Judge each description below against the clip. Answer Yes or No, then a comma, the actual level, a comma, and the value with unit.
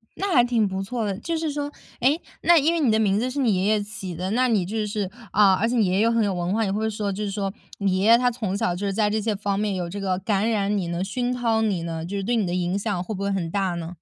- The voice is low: No, high, 205 Hz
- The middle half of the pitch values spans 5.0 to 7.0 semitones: No, average, 3.1 semitones